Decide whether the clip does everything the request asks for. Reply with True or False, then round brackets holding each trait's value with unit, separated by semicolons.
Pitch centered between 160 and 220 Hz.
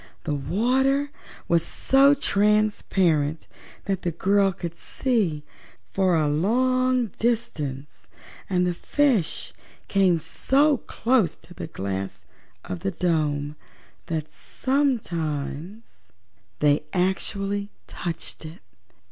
True (185 Hz)